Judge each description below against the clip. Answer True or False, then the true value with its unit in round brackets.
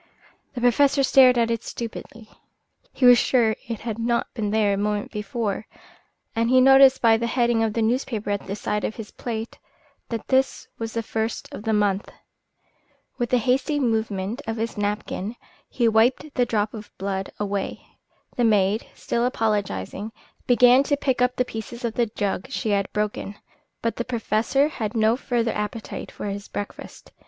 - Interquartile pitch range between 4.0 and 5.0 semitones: False (2.7 semitones)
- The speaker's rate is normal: True (175 wpm)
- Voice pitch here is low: False (225 Hz)